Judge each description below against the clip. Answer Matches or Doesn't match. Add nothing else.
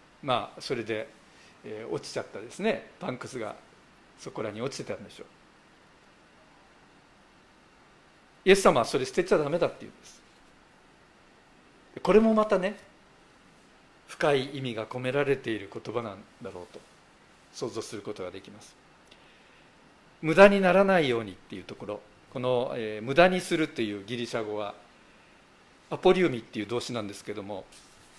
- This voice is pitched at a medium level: Doesn't match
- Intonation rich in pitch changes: Matches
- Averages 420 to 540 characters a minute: Doesn't match